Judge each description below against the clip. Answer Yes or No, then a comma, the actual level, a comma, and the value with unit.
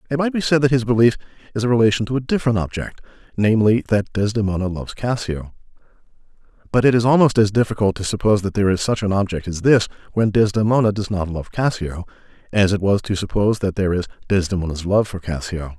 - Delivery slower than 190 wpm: No, average, 200 wpm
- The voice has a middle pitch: No, low, 105 Hz